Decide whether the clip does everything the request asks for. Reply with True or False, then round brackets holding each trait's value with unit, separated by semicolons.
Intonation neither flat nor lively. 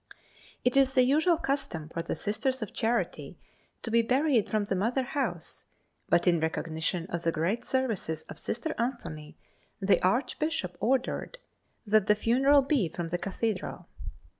False (6.9 semitones)